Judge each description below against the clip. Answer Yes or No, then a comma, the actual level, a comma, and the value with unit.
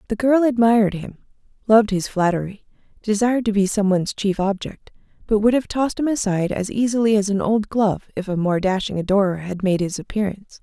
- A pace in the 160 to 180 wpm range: No, average, 200 wpm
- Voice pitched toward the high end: Yes, high, 205 Hz